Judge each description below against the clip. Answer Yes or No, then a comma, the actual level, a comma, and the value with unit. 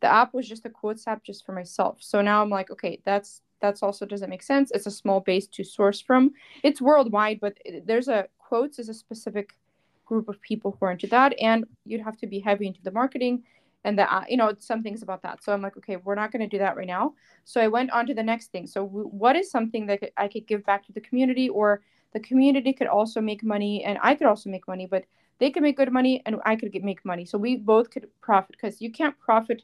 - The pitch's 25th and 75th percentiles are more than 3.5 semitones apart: No, average, 3.2 semitones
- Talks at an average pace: No, fast, 260 wpm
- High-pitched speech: Yes, high, 215 Hz